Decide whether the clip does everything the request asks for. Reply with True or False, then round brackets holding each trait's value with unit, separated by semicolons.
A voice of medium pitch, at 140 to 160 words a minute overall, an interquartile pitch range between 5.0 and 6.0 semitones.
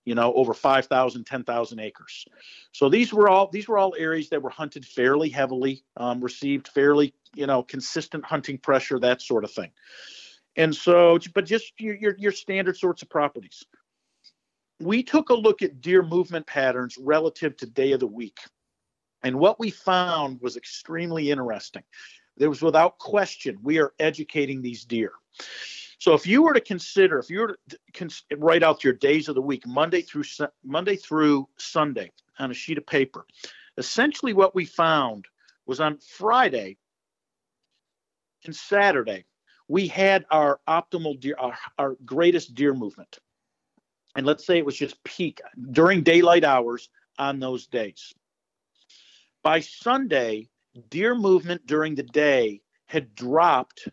True (155 Hz; 155 wpm; 5.5 semitones)